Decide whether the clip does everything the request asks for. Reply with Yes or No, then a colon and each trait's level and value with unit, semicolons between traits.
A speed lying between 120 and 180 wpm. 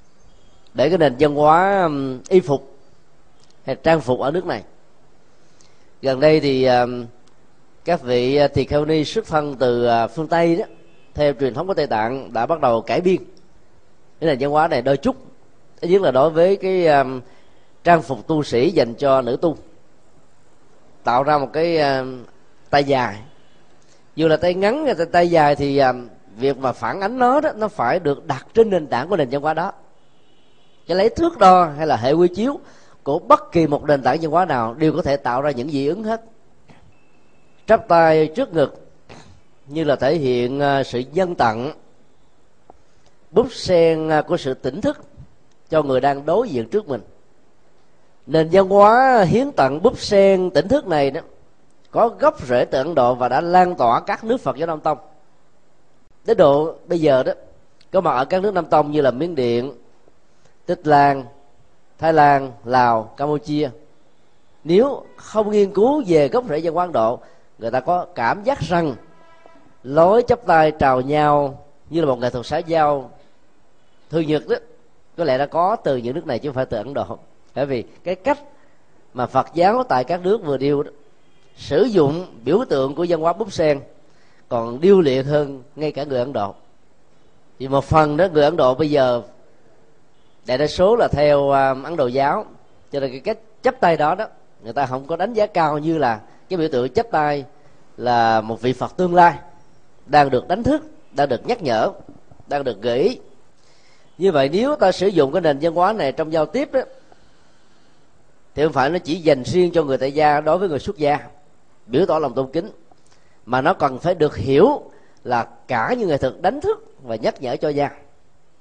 No: average, 190 wpm